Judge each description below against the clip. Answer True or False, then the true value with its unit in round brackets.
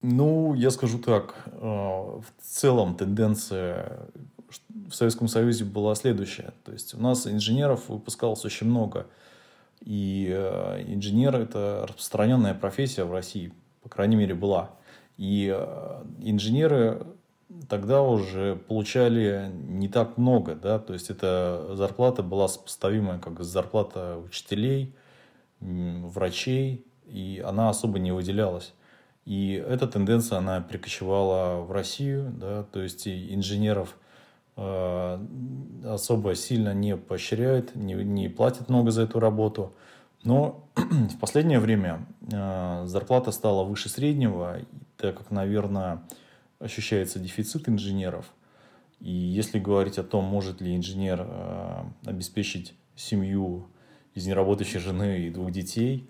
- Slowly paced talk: False (120 wpm)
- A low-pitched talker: True (105 Hz)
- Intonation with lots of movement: False (3.7 semitones)